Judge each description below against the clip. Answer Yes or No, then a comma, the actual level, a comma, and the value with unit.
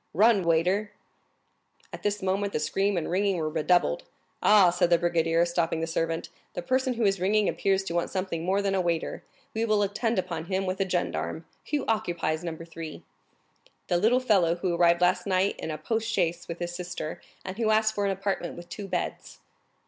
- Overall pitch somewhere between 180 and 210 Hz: Yes, medium, 185 Hz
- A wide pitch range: No, average, 3.2 semitones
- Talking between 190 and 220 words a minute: Yes, average, 200 wpm